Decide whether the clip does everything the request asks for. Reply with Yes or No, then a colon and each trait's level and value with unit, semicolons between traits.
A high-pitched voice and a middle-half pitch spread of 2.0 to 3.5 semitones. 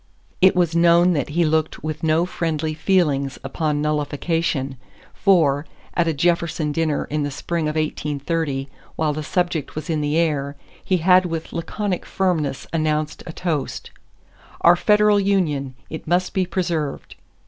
No: medium, 160 Hz; average, 2.8 semitones